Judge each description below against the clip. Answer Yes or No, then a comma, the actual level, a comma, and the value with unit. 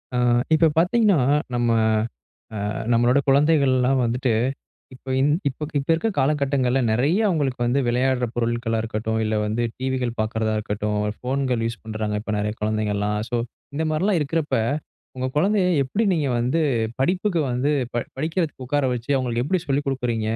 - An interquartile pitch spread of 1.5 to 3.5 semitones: No, average, 4.2 semitones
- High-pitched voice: No, low, 130 Hz